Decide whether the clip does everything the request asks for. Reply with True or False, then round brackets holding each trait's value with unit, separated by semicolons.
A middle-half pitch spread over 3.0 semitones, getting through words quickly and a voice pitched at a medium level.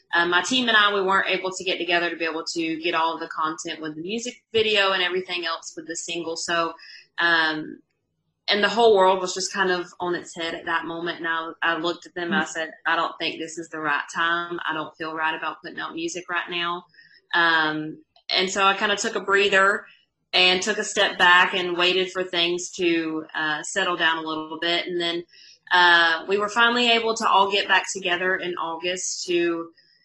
False (2.4 semitones; 225 wpm; 175 Hz)